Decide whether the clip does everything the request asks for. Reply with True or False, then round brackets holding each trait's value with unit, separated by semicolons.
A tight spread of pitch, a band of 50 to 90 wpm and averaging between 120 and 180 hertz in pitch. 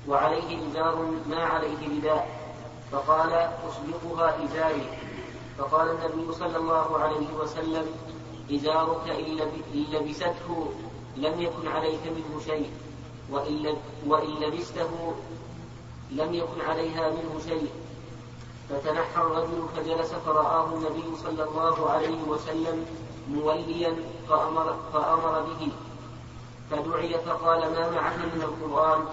False (1.2 semitones; 100 wpm; 160 Hz)